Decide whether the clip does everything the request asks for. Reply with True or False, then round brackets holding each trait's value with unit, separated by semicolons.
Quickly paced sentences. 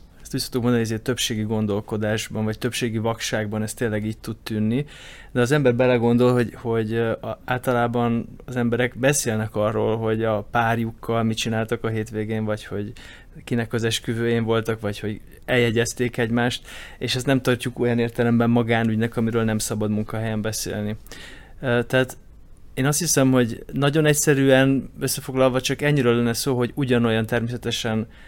False (145 wpm)